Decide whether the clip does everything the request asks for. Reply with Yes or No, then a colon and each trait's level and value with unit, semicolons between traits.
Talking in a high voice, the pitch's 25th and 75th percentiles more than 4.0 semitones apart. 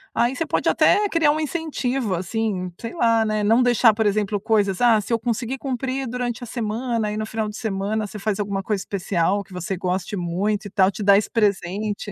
No: high, 215 Hz; average, 3.3 semitones